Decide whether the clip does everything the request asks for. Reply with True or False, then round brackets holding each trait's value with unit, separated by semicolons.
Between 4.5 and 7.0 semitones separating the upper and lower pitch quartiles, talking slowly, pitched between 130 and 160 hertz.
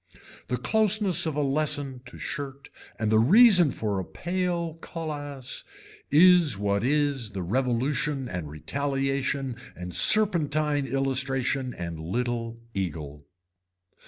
True (4.8 semitones; 115 wpm; 135 Hz)